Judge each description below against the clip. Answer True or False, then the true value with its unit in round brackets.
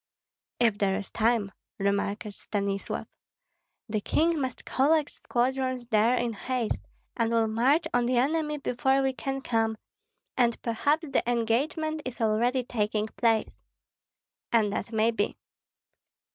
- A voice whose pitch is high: True (235 Hz)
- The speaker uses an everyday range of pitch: True (3.4 semitones)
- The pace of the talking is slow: True (130 wpm)